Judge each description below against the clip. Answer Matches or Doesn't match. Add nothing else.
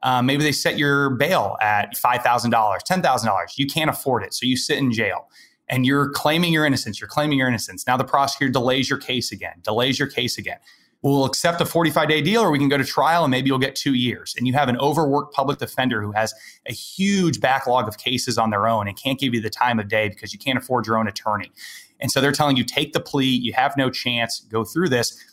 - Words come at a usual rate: Doesn't match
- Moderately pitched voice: Doesn't match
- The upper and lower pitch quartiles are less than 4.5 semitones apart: Matches